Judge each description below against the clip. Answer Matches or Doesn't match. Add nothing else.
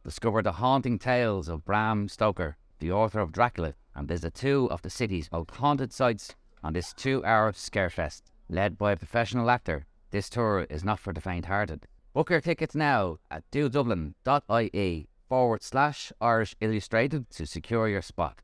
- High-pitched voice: Doesn't match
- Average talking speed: Matches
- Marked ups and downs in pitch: Matches